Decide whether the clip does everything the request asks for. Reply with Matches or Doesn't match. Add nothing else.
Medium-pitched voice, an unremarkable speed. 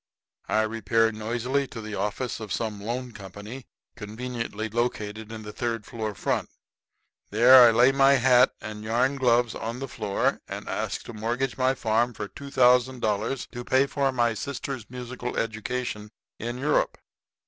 Doesn't match